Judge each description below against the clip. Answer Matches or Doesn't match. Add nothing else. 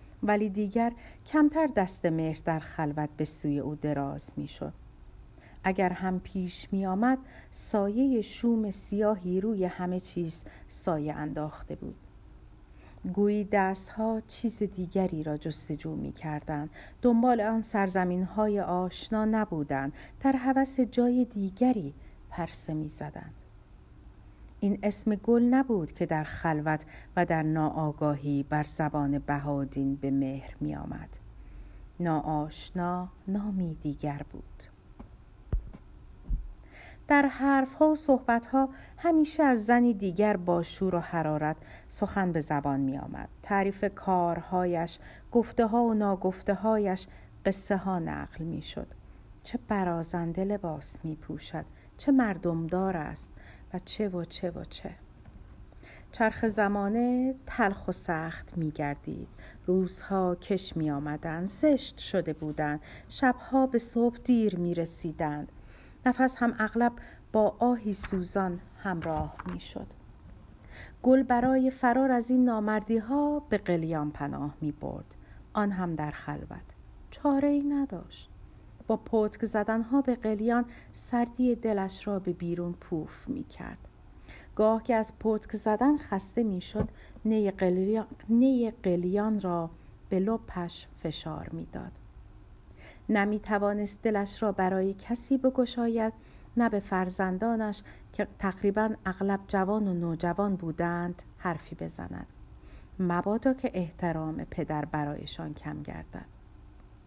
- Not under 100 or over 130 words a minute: Matches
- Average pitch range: Doesn't match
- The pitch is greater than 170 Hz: Matches